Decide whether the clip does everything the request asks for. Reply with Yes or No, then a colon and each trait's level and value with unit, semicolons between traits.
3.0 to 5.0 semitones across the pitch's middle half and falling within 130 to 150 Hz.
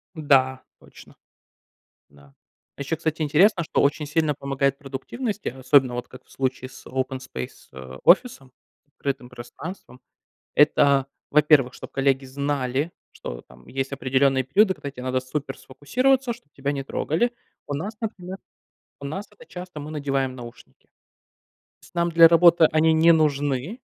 Yes: average, 3.6 semitones; medium, 140 Hz